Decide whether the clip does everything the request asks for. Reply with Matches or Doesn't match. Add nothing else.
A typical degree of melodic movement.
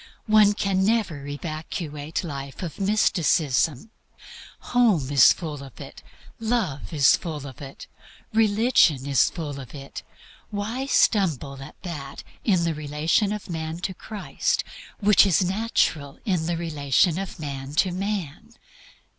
Doesn't match